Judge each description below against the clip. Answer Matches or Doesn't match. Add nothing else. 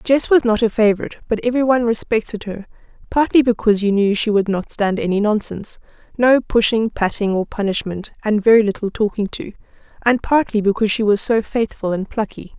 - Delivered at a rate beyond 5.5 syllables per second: Matches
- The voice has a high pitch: Matches